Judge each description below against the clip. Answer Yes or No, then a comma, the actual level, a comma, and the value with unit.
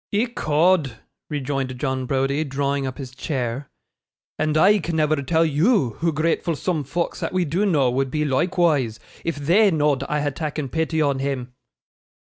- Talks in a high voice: No, medium, 150 Hz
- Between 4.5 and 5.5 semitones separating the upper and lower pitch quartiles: No, average, 3.5 semitones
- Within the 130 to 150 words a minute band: No, average, 165 wpm